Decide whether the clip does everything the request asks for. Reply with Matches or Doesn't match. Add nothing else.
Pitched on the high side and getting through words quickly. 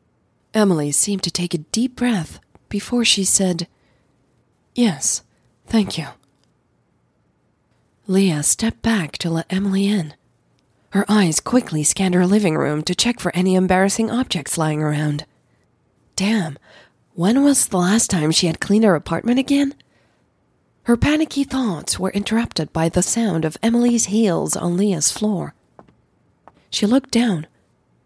Doesn't match